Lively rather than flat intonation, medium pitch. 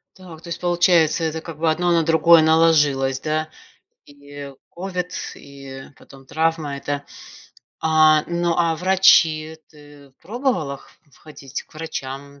No: average, 2.9 semitones; medium, 155 Hz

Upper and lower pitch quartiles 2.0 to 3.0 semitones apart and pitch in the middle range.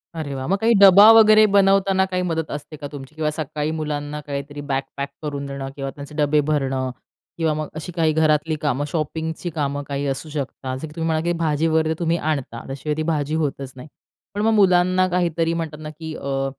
Yes: narrow, 2.6 semitones; medium, 155 Hz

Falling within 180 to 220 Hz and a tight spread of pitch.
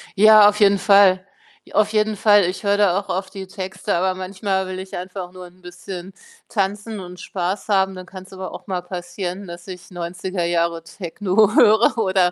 Yes: high, 190 Hz; narrow, 1.9 semitones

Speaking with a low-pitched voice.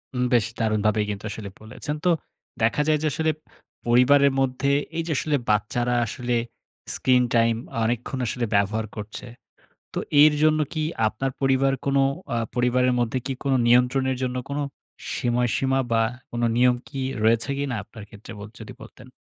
Yes: low, 125 Hz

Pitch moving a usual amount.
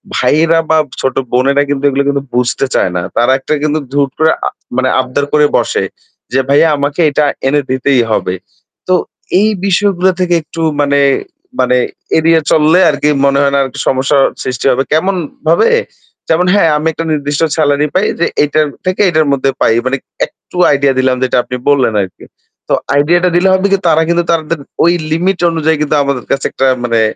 Yes: average, 3.4 semitones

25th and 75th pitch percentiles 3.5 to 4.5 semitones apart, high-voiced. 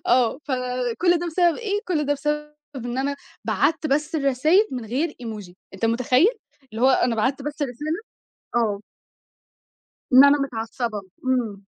Yes: average, 3.9 semitones; very high, 265 Hz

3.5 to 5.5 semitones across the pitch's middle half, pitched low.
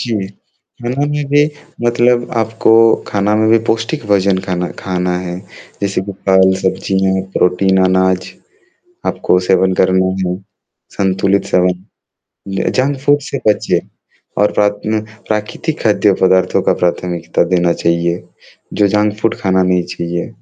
No: average, 2.8 semitones; very low, 95 Hz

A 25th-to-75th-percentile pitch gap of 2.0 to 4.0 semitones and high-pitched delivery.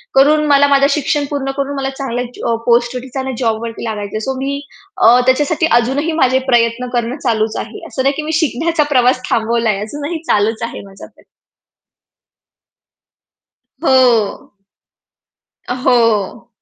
Yes: average, 3.3 semitones; very high, 250 Hz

